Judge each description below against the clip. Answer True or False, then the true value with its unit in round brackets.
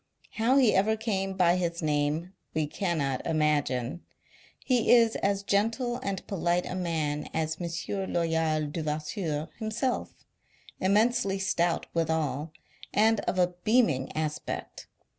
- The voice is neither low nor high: True (175 Hz)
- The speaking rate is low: True (125 wpm)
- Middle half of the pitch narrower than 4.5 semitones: False (4.8 semitones)